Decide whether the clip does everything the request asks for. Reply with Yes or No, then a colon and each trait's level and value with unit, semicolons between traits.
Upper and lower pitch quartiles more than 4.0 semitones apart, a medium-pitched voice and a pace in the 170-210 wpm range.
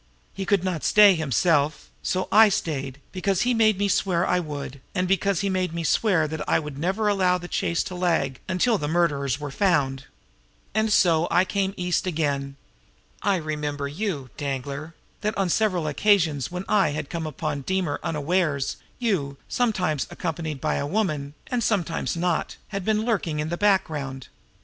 Yes: average, 4.7 semitones; medium, 170 Hz; average, 175 wpm